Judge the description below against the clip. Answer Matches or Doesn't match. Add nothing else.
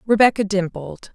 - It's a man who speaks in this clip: Doesn't match